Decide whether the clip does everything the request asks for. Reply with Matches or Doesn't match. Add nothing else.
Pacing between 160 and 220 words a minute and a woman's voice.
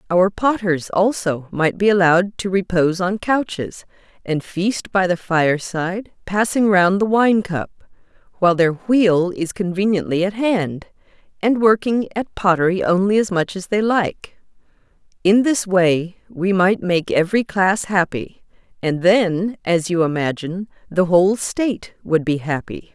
Doesn't match